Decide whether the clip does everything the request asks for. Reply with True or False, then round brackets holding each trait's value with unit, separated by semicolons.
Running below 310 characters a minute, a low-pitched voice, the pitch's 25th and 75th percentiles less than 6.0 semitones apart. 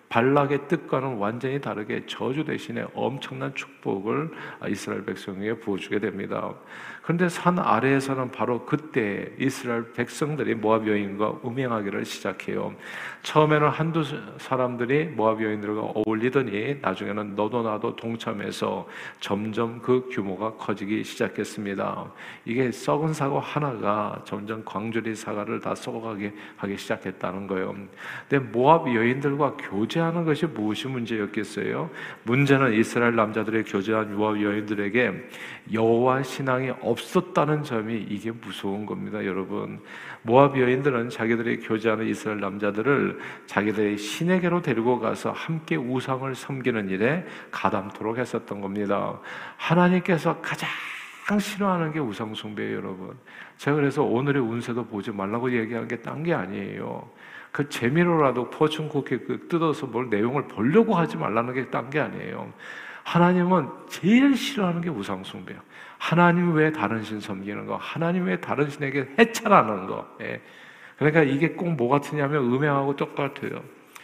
False (335 characters per minute; 120 Hz; 5.4 semitones)